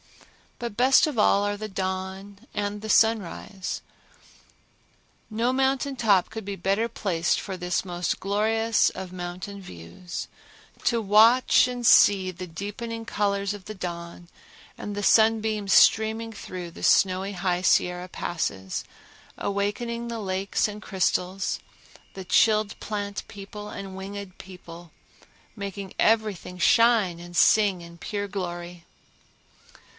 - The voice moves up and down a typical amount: Yes, average, 3.0 semitones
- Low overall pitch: No, high, 200 Hz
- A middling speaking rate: No, slow, 130 wpm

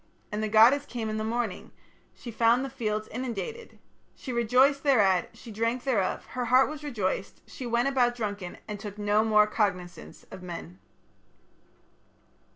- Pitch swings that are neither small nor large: Yes, average, 3.4 semitones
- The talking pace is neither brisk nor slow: Yes, average, 160 wpm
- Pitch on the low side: No, high, 225 Hz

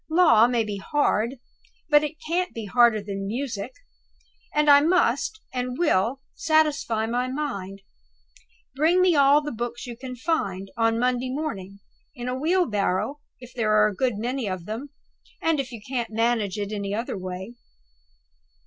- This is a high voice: Yes, high, 245 Hz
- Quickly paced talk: No, average, 165 wpm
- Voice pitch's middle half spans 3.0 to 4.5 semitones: No, wide, 5.4 semitones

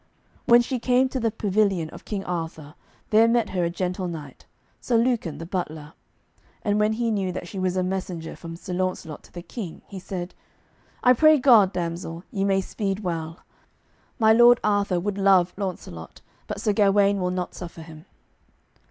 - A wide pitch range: No, average, 3.7 semitones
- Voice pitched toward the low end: No, high, 190 Hz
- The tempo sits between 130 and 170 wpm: No, average, 180 wpm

